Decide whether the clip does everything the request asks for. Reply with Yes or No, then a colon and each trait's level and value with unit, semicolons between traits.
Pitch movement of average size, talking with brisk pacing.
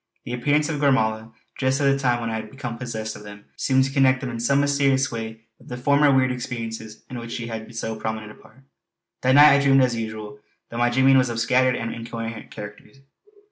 Yes: average, 3.1 semitones; fast, 230 wpm